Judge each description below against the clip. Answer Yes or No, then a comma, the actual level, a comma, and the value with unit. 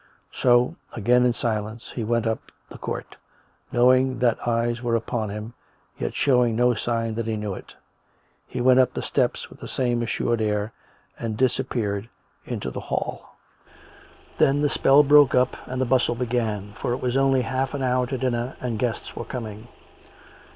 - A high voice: No, low, 120 Hz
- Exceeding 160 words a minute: Yes, average, 180 wpm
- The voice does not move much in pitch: Yes, narrow, 2.3 semitones